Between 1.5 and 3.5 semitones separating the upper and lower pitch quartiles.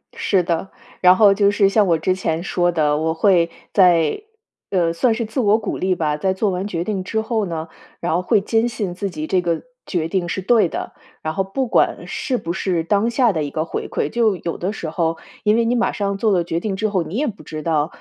No: average, 4.1 semitones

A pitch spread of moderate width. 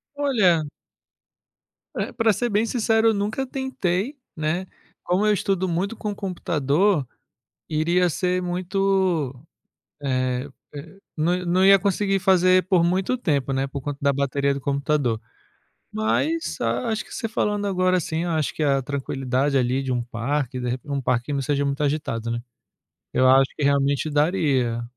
No: wide, 5.9 semitones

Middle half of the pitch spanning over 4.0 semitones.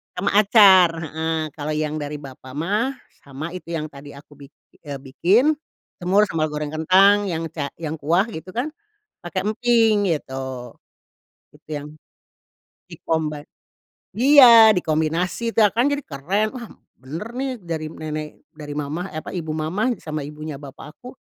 Yes: wide, 5.5 semitones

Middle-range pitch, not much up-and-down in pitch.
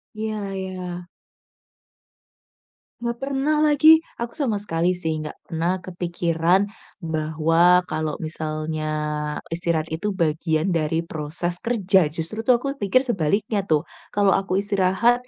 No: medium, 180 Hz; average, 4.4 semitones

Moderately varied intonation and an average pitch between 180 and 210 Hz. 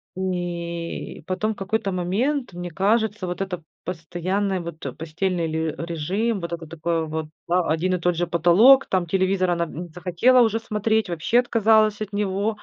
Yes: average, 3.7 semitones; medium, 185 Hz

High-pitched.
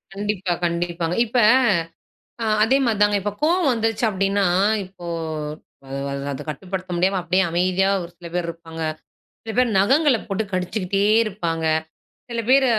Yes: high, 195 Hz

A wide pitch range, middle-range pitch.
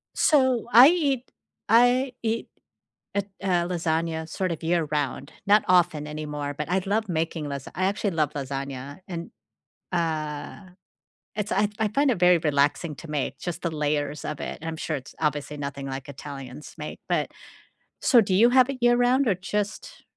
Yes: wide, 6.0 semitones; medium, 165 Hz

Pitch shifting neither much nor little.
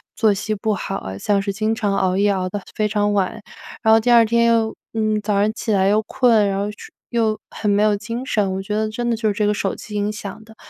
No: narrow, 1.7 semitones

